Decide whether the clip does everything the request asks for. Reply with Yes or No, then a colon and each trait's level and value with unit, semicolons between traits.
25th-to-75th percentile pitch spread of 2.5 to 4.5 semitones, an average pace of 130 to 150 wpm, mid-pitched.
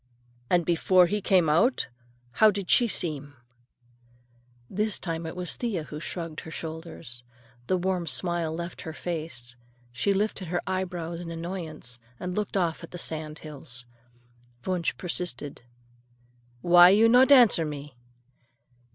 Yes: average, 3.1 semitones; average, 140 wpm; medium, 170 Hz